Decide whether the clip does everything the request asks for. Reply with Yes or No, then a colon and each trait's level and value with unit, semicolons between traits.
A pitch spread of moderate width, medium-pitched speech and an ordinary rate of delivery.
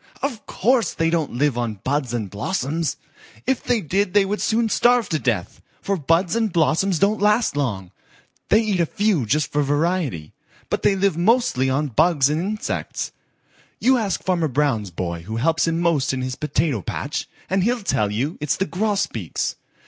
No: wide, 7.2 semitones; medium, 165 Hz; average, 180 wpm